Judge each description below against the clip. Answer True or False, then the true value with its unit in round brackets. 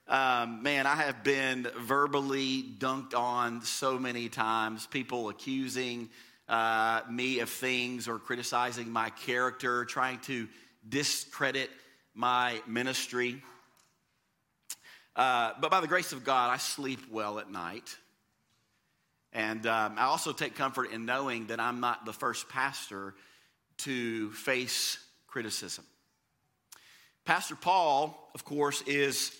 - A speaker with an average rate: False (120 wpm)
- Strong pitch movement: False (2.7 semitones)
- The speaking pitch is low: True (125 Hz)